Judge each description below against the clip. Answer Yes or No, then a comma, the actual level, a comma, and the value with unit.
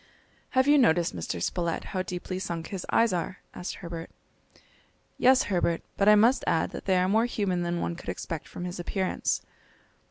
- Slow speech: No, average, 185 wpm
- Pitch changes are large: No, average, 3.3 semitones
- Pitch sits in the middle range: Yes, medium, 180 Hz